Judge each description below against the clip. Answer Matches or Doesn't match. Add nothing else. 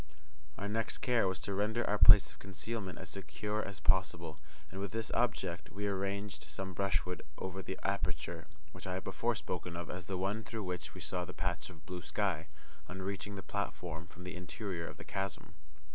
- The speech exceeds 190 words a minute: Matches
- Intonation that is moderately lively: Doesn't match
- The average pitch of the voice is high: Doesn't match